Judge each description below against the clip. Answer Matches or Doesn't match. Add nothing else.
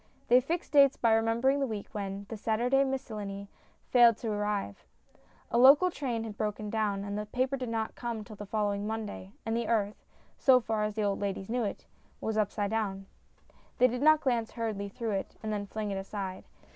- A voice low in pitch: Doesn't match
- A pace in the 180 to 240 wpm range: Matches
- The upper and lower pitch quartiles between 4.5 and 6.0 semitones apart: Doesn't match